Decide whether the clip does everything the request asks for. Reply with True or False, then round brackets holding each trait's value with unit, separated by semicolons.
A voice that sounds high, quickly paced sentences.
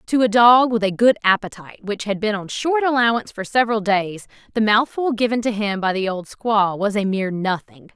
True (215 Hz; 220 wpm)